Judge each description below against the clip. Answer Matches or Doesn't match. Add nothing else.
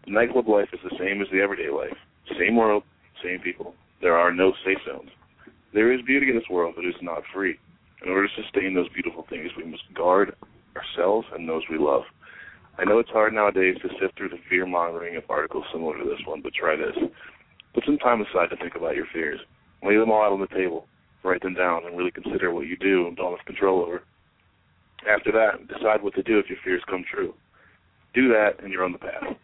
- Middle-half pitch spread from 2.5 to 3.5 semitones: Matches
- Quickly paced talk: Matches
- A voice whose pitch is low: Matches